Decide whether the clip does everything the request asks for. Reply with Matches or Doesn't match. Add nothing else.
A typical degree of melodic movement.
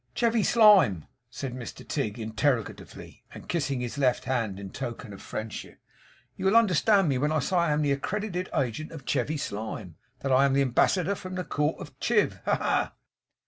Doesn't match